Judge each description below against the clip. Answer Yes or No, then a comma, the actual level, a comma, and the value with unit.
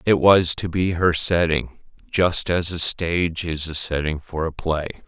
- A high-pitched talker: No, very low, 85 Hz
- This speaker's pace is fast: No, average, 190 wpm